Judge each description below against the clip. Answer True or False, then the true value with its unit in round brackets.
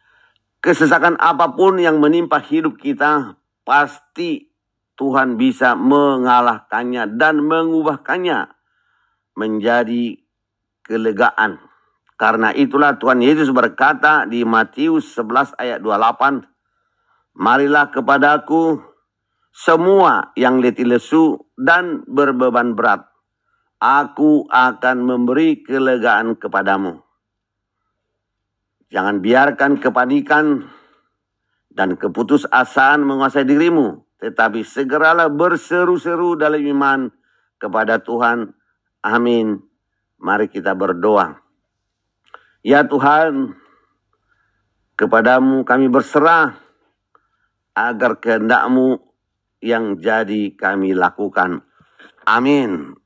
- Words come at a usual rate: False (80 wpm)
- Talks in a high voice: False (135 Hz)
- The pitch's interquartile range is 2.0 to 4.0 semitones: False (5.1 semitones)